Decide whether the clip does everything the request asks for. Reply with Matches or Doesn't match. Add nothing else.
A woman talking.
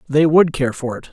Doesn't match